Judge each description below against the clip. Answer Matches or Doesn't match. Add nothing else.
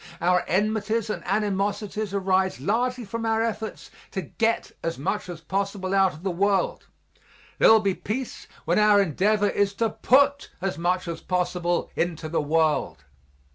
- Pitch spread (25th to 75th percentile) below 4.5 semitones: Matches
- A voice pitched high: Matches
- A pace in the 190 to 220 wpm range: Doesn't match